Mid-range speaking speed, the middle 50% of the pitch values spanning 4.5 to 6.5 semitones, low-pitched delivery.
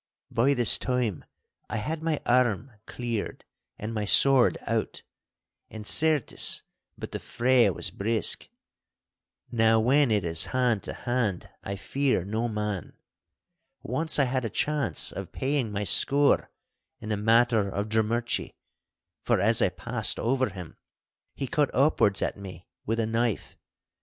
No: average, 145 wpm; average, 3.7 semitones; low, 115 Hz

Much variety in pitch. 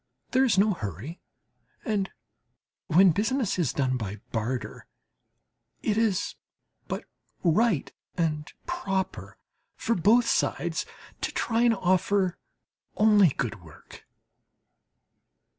Yes: wide, 6.5 semitones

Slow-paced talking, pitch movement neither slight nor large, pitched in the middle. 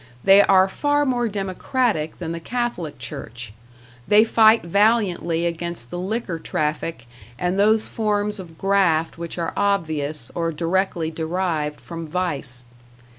Yes: slow, 130 wpm; average, 4.2 semitones; medium, 175 Hz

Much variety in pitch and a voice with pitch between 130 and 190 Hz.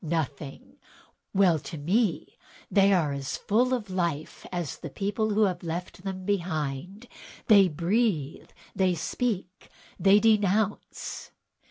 No: average, 4.2 semitones; medium, 185 Hz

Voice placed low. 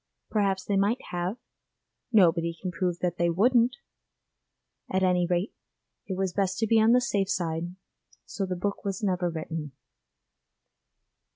No: medium, 185 Hz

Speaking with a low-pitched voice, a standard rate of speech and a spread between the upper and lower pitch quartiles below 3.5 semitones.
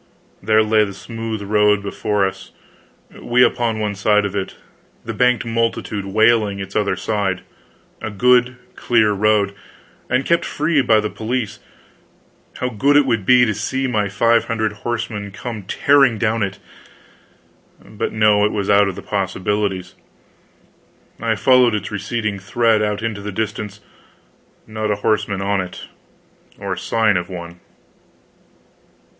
Yes: low, 105 Hz; average, 145 wpm; narrow, 2.4 semitones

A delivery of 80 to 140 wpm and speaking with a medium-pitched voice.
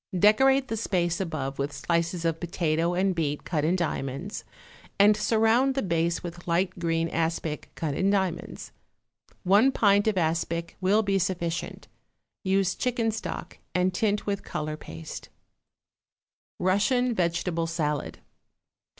Yes: slow, 135 wpm; medium, 180 Hz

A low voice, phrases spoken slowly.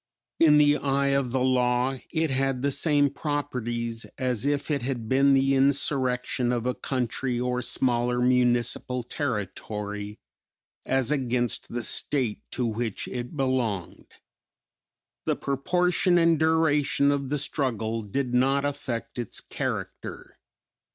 Yes: low, 130 Hz; slow, 130 wpm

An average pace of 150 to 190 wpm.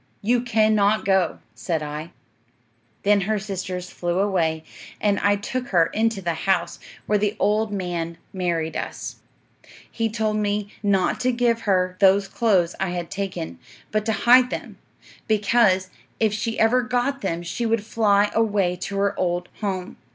Yes: average, 160 wpm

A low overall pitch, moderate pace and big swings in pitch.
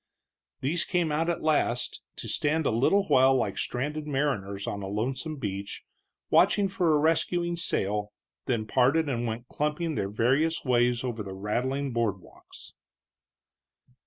Yes: low, 130 Hz; average, 150 wpm; wide, 5.7 semitones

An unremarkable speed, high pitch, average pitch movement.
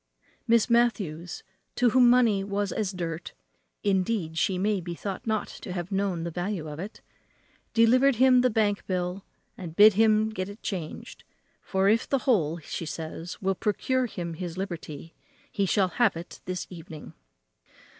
Yes: average, 165 wpm; high, 195 Hz; average, 4.0 semitones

